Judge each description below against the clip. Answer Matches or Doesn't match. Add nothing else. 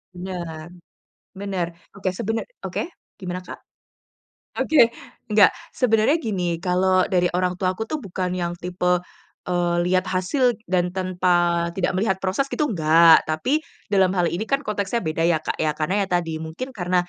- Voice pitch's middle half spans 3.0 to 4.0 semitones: Doesn't match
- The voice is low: Doesn't match